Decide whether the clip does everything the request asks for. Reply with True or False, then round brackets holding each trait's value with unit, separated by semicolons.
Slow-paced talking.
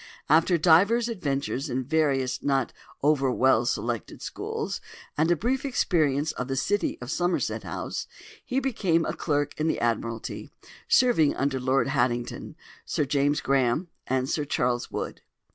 False (150 wpm)